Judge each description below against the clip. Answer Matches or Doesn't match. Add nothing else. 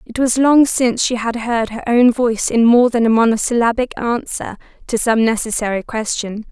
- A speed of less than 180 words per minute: Doesn't match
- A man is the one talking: Doesn't match